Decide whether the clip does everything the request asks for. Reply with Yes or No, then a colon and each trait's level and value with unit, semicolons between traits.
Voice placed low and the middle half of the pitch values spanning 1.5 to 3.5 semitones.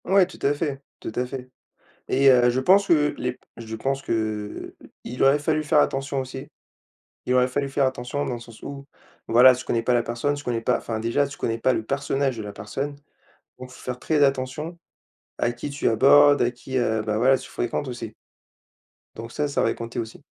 Yes: low, 130 Hz; average, 3.2 semitones